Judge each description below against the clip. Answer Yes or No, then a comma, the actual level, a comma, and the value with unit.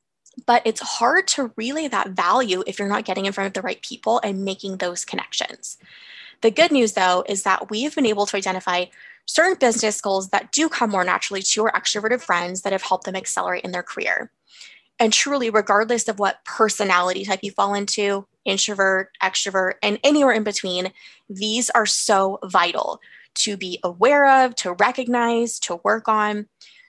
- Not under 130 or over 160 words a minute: No, average, 180 wpm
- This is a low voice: No, high, 210 Hz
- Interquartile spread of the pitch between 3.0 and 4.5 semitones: Yes, average, 3.5 semitones